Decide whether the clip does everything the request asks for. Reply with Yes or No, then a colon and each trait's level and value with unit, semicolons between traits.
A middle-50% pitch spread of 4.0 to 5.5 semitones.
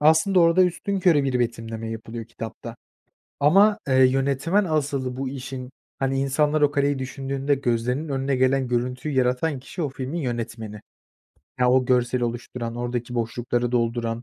No: average, 3.0 semitones